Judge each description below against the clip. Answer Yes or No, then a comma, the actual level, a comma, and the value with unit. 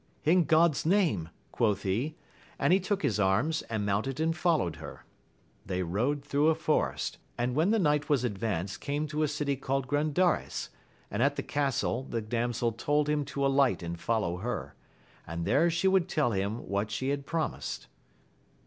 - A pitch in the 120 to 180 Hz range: Yes, medium, 140 Hz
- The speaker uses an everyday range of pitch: No, wide, 6.0 semitones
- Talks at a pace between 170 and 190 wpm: Yes, average, 180 wpm